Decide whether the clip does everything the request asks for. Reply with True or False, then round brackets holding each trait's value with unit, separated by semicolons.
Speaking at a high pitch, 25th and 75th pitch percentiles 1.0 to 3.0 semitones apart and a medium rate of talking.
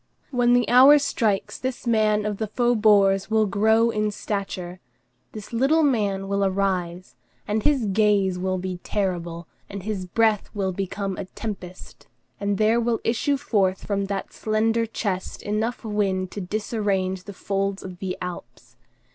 True (205 Hz; 2.7 semitones; 155 wpm)